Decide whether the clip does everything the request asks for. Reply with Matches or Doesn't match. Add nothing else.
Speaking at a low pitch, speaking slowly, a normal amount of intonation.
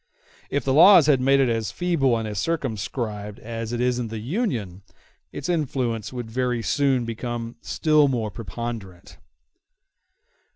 Doesn't match